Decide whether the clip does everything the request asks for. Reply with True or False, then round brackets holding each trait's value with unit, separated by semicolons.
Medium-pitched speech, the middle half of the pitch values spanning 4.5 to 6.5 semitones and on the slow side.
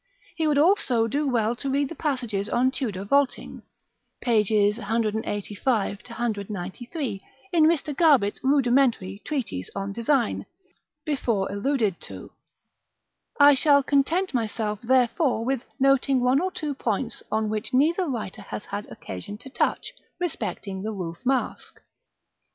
False (240 Hz; 5.0 semitones; 130 wpm)